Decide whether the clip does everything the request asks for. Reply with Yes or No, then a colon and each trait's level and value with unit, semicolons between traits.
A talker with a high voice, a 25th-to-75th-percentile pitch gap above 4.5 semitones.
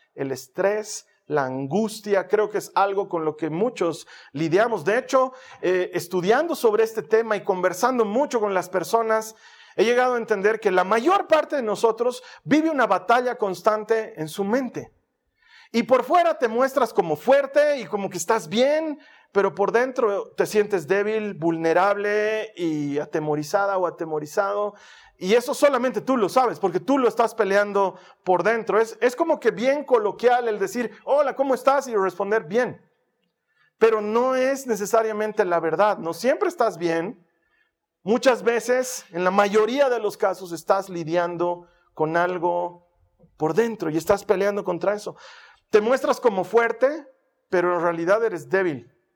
Yes: high, 215 Hz; average, 5.3 semitones